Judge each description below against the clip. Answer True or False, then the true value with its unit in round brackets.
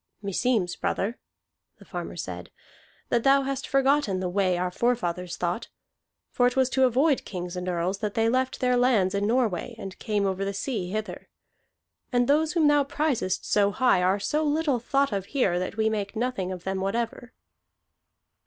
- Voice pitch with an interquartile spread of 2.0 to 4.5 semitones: False (5.5 semitones)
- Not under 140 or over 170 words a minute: False (180 wpm)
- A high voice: True (220 Hz)